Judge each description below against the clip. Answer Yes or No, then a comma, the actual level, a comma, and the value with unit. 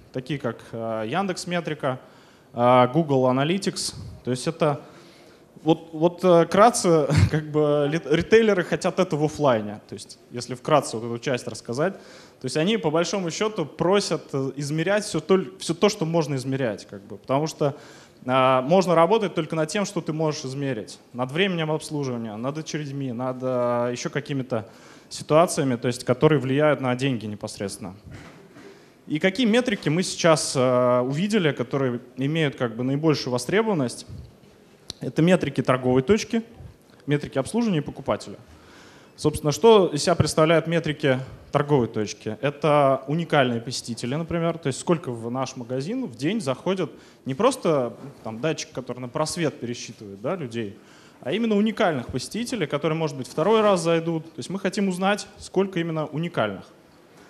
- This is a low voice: No, medium, 150 Hz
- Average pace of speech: Yes, average, 150 wpm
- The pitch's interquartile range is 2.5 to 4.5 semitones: No, average, 4.9 semitones